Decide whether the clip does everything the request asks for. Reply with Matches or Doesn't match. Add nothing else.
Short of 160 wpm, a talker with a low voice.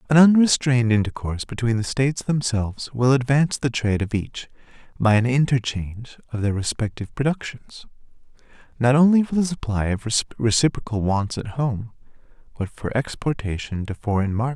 Matches